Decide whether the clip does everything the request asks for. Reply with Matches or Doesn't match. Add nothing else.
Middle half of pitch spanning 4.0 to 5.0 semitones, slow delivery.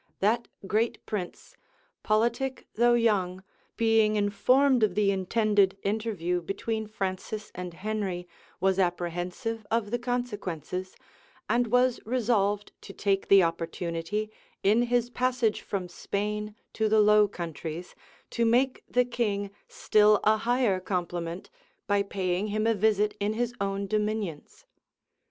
Doesn't match